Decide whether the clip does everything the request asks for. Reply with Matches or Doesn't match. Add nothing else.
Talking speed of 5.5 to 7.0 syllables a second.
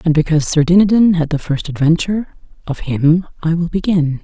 Matches